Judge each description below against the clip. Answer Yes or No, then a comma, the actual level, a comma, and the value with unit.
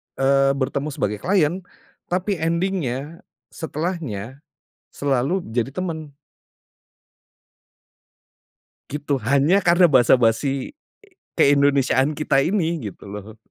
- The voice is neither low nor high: Yes, medium, 145 Hz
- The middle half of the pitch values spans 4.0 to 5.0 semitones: Yes, average, 4.3 semitones